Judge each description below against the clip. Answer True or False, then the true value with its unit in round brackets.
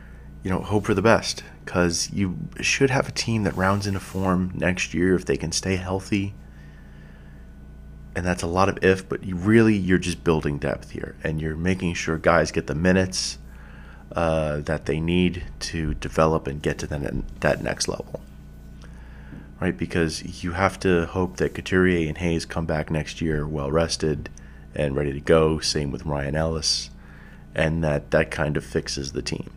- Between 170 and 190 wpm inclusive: True (185 wpm)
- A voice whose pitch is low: True (80 Hz)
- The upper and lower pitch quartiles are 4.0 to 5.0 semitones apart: True (4.3 semitones)